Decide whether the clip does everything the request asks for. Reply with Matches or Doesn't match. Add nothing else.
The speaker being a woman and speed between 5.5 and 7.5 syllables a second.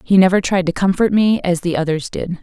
Matches